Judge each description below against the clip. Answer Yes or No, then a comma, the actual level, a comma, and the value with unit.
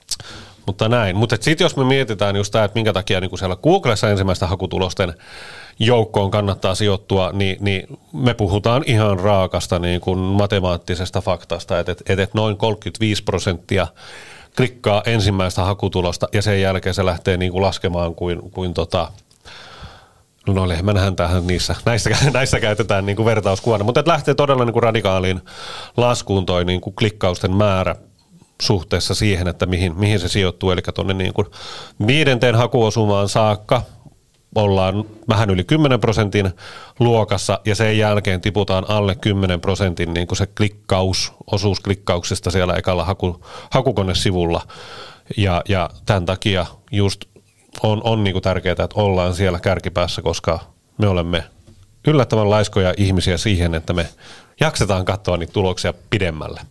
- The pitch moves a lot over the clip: No, average, 2.9 semitones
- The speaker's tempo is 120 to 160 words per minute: Yes, average, 140 wpm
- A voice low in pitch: Yes, low, 100 Hz